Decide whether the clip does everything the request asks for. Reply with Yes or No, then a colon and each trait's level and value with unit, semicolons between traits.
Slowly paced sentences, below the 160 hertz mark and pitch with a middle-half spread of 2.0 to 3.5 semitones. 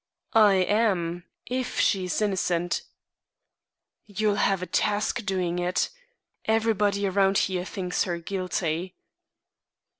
No: slow, 110 wpm; high, 195 Hz; narrow, 2.6 semitones